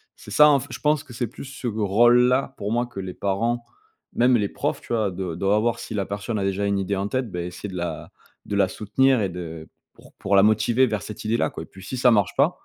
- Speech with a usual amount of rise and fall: Yes, average, 3.8 semitones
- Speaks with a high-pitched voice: No, low, 105 Hz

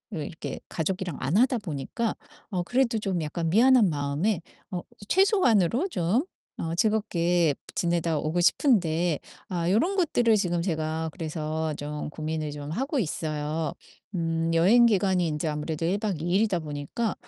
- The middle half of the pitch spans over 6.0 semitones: No, wide, 5.4 semitones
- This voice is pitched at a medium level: Yes, medium, 170 Hz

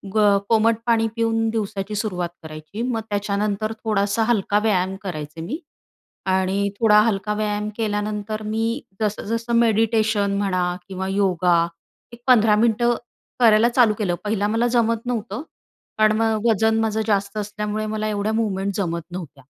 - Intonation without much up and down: Yes, narrow, 2.1 semitones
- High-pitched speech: Yes, high, 210 Hz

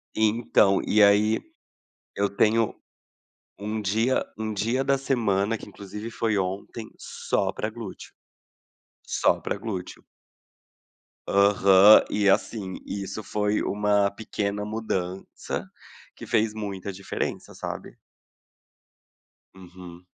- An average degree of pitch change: No, narrow, 1.9 semitones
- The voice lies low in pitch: Yes, low, 105 Hz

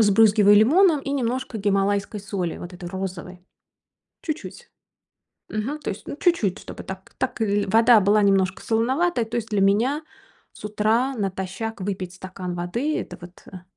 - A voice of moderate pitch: No, high, 205 Hz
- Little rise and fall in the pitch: No, average, 3.9 semitones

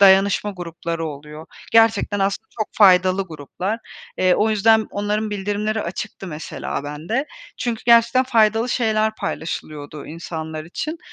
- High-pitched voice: Yes, high, 200 Hz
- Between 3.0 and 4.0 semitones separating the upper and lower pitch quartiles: No, average, 4.9 semitones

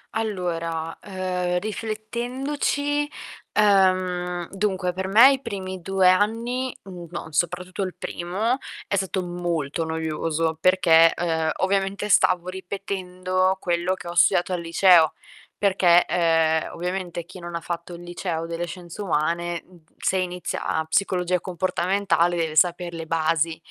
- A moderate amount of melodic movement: No, narrow, 2.3 semitones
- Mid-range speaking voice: Yes, medium, 180 Hz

